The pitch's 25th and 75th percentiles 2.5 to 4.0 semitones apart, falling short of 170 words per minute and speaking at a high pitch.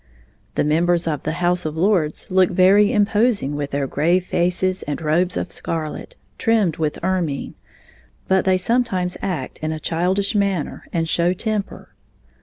No: average, 3.6 semitones; average, 155 wpm; medium, 180 Hz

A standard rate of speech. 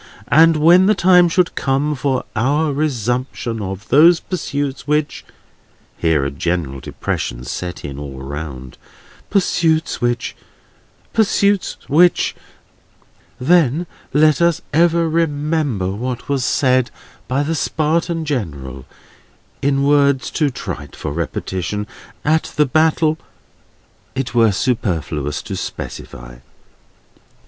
No: slow, 110 wpm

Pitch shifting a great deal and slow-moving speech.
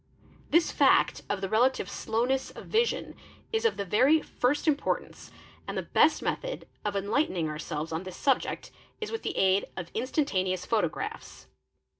No: wide, 7.9 semitones; average, 160 wpm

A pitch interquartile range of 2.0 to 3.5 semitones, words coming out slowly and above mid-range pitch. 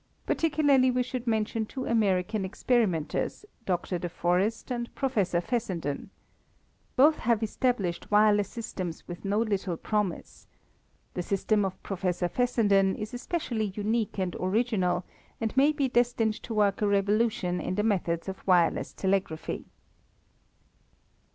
No: average, 4.2 semitones; slow, 130 wpm; high, 210 Hz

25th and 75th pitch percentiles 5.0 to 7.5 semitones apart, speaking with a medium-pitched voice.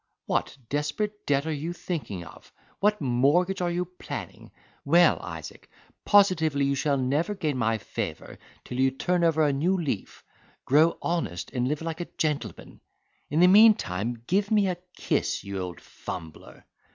Yes: wide, 5.4 semitones; medium, 155 Hz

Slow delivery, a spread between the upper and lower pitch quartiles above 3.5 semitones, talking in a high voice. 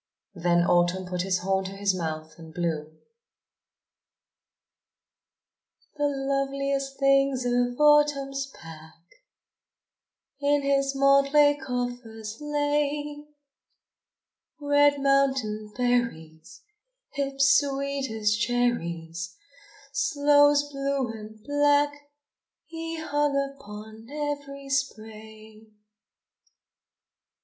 Yes: slow, 80 wpm; average, 5.2 semitones; very high, 270 Hz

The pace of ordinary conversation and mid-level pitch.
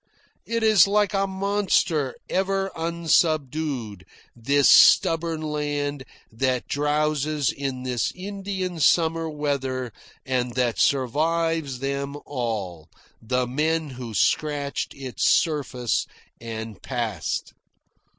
No: slow, 100 wpm; medium, 145 Hz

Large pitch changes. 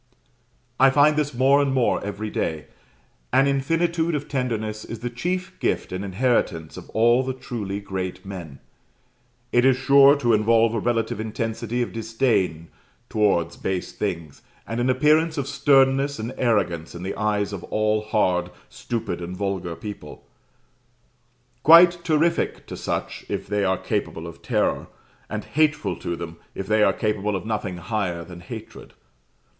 Yes: wide, 5.7 semitones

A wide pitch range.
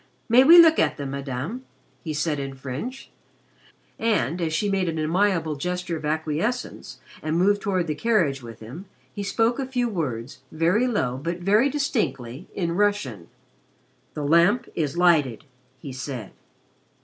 Yes: wide, 6.8 semitones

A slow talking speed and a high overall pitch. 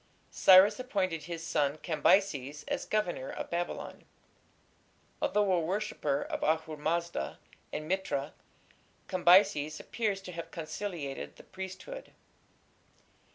No: slow, 110 wpm; medium, 170 Hz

